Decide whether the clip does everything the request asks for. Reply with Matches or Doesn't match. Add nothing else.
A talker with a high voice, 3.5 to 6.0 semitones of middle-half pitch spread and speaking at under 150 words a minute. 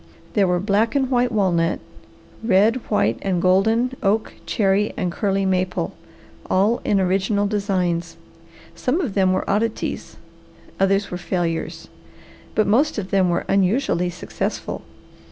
Doesn't match